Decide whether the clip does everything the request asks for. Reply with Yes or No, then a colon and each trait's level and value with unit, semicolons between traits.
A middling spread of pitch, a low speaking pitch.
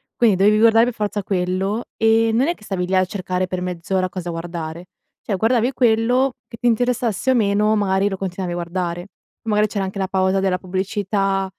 No: average, 3.3 semitones; high, 195 Hz